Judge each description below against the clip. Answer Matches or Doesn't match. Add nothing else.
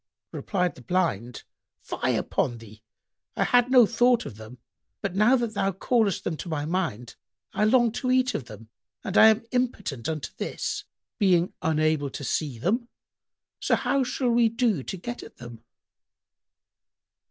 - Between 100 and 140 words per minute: Doesn't match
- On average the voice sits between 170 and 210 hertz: Matches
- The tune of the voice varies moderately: Doesn't match